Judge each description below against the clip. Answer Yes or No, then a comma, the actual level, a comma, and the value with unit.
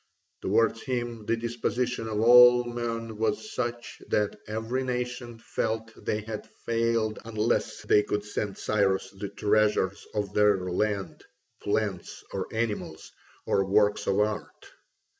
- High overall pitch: No, low, 110 Hz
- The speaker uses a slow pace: Yes, slow, 130 wpm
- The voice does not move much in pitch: Yes, narrow, 2.2 semitones